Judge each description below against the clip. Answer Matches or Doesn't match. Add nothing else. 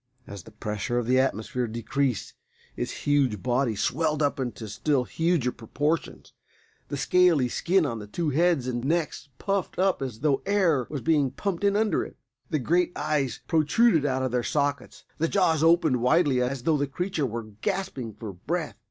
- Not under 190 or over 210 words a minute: Doesn't match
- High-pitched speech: Doesn't match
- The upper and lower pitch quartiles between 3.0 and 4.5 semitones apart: Doesn't match